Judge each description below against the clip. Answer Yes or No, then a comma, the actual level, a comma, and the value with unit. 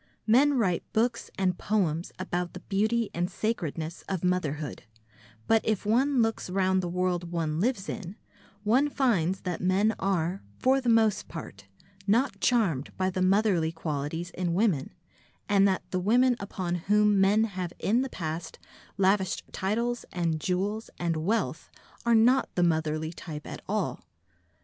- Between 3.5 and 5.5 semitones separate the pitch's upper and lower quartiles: Yes, average, 4.3 semitones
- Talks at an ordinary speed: Yes, average, 155 wpm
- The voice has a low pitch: No, high, 190 Hz